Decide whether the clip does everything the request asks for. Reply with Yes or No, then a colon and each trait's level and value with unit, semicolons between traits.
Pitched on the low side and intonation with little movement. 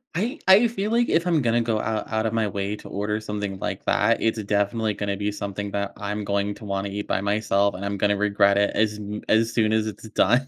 Yes: low, 105 Hz; narrow, 1.9 semitones